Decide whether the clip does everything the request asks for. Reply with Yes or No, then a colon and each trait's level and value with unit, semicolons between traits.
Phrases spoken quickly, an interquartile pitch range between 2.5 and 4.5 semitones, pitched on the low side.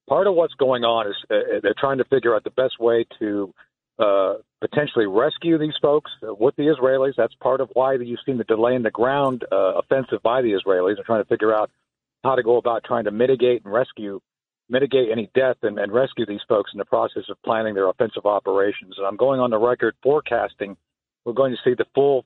Yes: fast, 220 wpm; average, 3.4 semitones; low, 125 Hz